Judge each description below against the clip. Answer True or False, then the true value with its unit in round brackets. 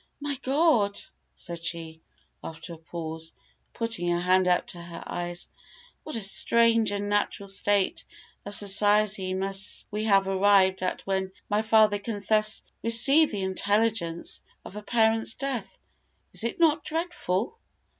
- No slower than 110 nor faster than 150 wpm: True (140 wpm)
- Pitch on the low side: False (205 Hz)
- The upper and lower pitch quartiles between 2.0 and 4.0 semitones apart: True (3.3 semitones)